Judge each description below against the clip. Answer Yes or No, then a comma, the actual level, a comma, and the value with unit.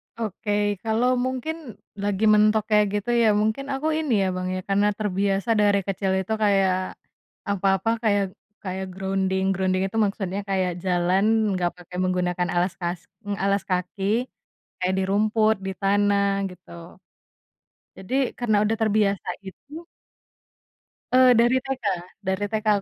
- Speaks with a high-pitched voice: Yes, high, 200 Hz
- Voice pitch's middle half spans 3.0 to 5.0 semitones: No, narrow, 2.4 semitones